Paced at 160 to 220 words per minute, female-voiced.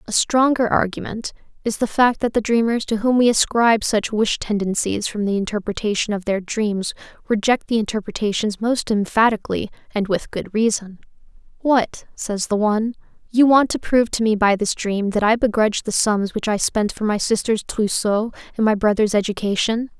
Yes: average, 180 wpm; female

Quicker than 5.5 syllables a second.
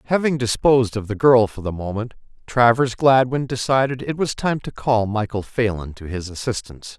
No: 5.2 syllables/s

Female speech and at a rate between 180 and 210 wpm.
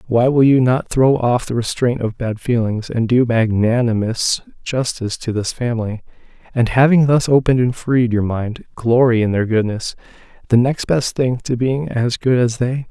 No: male; average, 185 wpm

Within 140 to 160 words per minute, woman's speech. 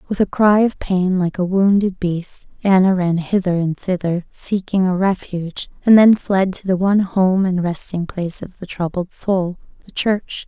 No: average, 185 wpm; female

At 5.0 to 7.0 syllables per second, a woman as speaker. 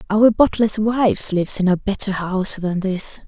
No: 4.6 syllables/s; female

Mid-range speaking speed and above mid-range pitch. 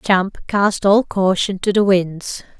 Yes: average, 160 wpm; high, 195 Hz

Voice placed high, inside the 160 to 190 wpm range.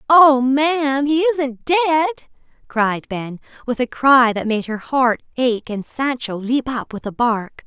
Yes: very high, 260 Hz; average, 170 wpm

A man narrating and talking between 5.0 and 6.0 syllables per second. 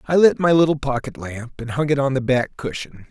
Yes: male; 5.4 syllables/s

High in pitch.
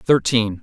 No: low, 115 Hz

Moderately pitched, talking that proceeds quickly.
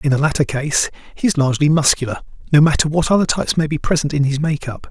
Yes: medium, 150 Hz; fast, 230 wpm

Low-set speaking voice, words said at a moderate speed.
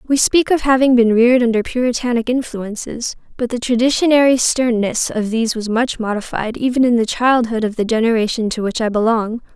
No: high, 235 Hz; average, 180 wpm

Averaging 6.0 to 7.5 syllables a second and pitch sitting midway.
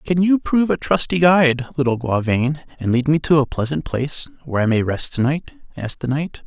Yes: 6.1 syllables/s; medium, 145 Hz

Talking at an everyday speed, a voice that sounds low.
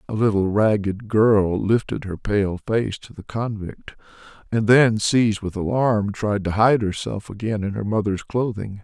Yes: average, 170 wpm; low, 105 Hz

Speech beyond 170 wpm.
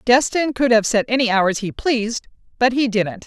Yes: average, 200 wpm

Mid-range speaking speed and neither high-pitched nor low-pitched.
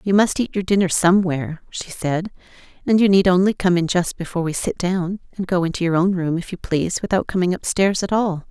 No: fast, 235 wpm; medium, 180 Hz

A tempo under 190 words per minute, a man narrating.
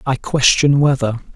Yes: slow, 135 wpm; male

